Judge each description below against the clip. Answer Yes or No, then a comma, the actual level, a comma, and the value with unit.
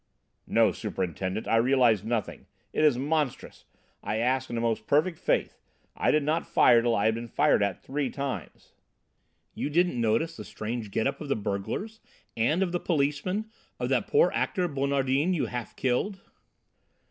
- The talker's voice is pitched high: No, low, 130 Hz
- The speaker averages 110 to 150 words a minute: No, average, 175 wpm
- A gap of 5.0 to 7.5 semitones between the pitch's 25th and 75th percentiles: Yes, wide, 5.4 semitones